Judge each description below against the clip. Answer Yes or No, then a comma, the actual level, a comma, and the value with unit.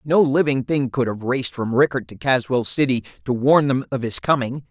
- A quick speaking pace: Yes, fast, 215 wpm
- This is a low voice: Yes, low, 130 Hz